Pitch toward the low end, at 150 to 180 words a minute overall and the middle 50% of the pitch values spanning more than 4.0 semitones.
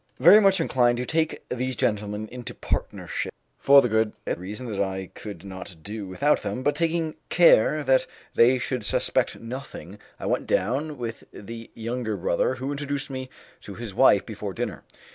Yes: low, 125 Hz; average, 170 wpm; average, 4.9 semitones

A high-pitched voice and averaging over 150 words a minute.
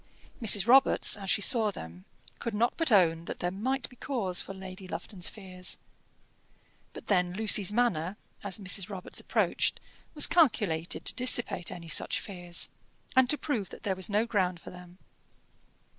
Yes: high, 195 Hz; average, 165 wpm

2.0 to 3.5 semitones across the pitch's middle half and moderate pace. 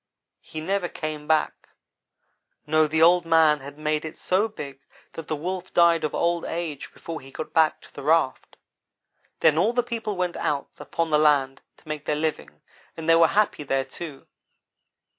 Yes: narrow, 2.4 semitones; average, 180 wpm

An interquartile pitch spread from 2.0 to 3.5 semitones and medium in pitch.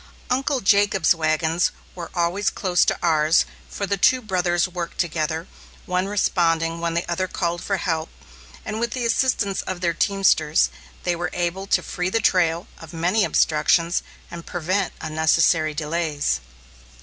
Yes: average, 2.9 semitones; medium, 175 Hz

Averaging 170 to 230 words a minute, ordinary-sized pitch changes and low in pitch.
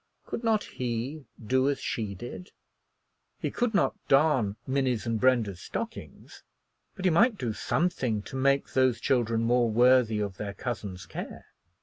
No: average, 150 wpm; average, 3.9 semitones; low, 125 Hz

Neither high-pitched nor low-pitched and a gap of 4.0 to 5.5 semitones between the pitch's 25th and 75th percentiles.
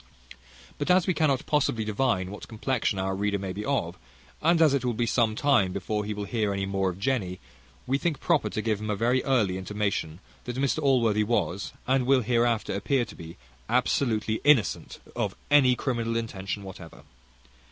No: low, 115 Hz; average, 4.8 semitones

